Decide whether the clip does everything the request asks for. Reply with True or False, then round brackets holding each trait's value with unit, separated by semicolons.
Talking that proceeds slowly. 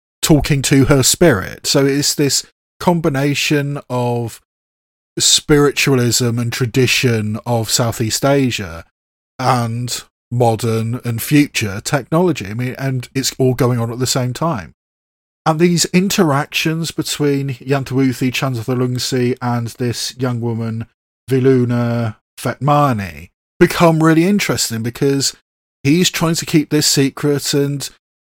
True (115 wpm)